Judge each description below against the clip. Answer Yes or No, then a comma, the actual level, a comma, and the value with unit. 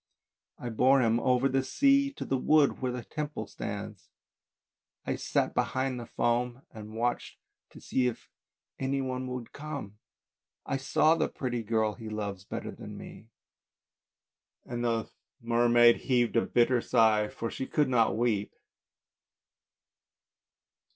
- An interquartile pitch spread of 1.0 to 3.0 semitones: Yes, narrow, 2.5 semitones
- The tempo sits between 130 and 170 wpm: Yes, average, 145 wpm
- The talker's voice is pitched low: Yes, low, 120 Hz